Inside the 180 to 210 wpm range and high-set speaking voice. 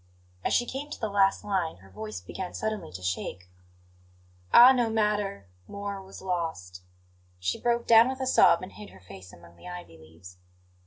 No: average, 190 wpm; medium, 180 Hz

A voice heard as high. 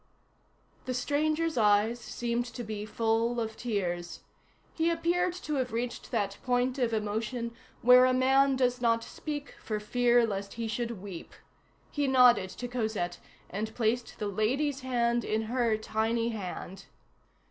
Yes: high, 235 Hz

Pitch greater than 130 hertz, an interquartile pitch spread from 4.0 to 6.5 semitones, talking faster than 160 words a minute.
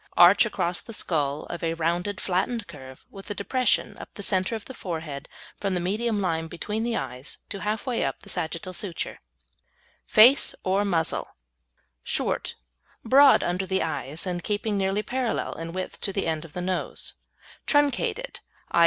Yes: high, 190 Hz; average, 4.4 semitones; average, 170 wpm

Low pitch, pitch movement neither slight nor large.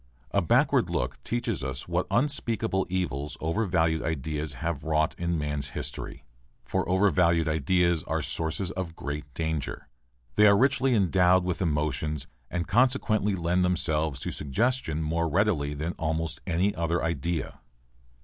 Yes: very low, 85 Hz; average, 3.5 semitones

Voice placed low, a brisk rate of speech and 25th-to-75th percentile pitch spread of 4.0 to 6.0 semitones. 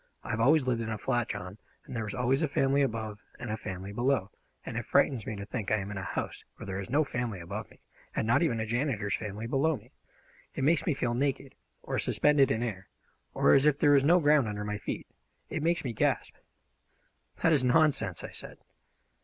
Yes: low, 120 Hz; fast, 225 wpm; average, 5.1 semitones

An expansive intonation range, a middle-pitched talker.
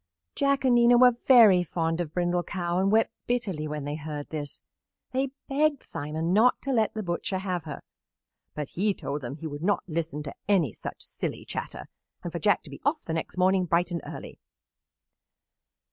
Yes: wide, 6.0 semitones; medium, 180 Hz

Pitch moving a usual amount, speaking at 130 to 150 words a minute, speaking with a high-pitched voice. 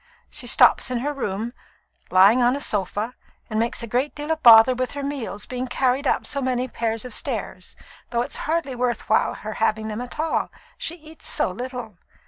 No: average, 3.8 semitones; average, 195 wpm; high, 245 Hz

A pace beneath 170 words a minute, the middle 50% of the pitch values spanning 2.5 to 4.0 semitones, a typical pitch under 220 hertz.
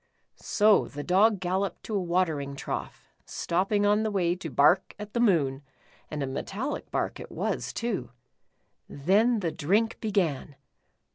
No: average, 155 wpm; average, 5.3 semitones; medium, 185 Hz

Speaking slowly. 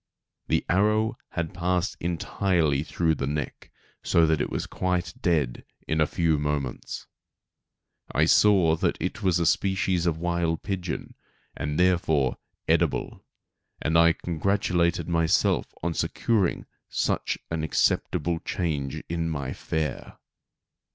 Yes: slow, 125 wpm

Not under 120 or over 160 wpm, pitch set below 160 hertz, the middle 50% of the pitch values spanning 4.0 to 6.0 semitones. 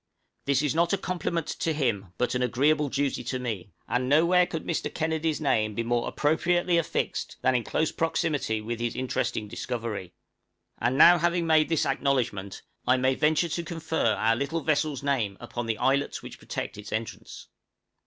No: average, 175 wpm; medium, 140 Hz; average, 5.3 semitones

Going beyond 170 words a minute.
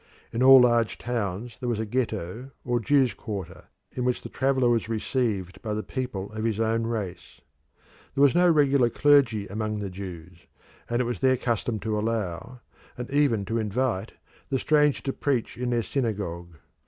Yes: average, 180 wpm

